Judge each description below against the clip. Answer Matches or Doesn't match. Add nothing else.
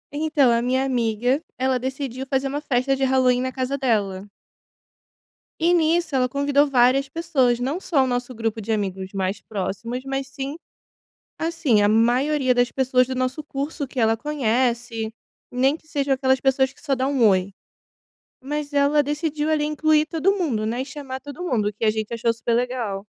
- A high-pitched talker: Matches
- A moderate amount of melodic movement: Matches